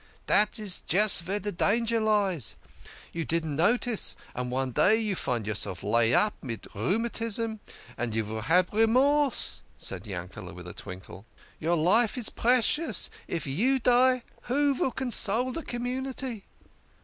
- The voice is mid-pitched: No, high, 205 Hz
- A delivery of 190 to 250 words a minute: No, average, 150 wpm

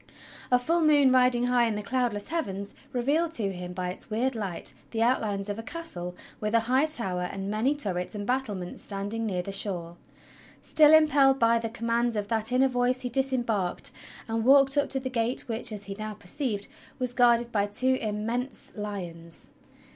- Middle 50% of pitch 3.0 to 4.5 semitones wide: Yes, average, 4.1 semitones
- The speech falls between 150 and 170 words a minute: No, average, 185 wpm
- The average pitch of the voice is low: No, high, 230 Hz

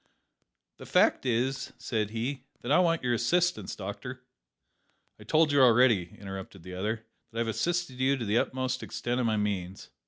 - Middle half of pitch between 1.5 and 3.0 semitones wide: No, average, 3.9 semitones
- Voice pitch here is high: No, low, 120 Hz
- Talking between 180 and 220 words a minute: Yes, average, 185 wpm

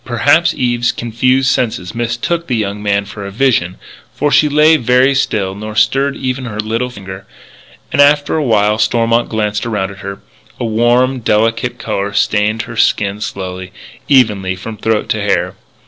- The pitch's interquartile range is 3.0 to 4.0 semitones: Yes, average, 3.7 semitones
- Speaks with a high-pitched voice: No, low, 115 Hz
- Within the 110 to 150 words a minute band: No, average, 160 wpm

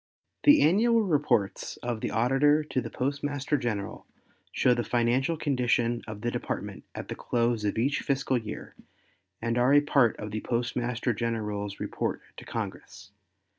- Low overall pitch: Yes, low, 120 Hz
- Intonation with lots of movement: No, average, 3.7 semitones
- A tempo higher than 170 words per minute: No, average, 155 wpm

